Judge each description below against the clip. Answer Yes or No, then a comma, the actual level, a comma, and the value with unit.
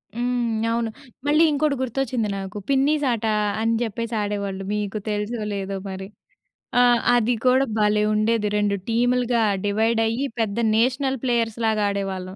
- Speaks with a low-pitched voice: No, high, 225 Hz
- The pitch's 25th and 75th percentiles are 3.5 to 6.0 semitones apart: No, average, 3.0 semitones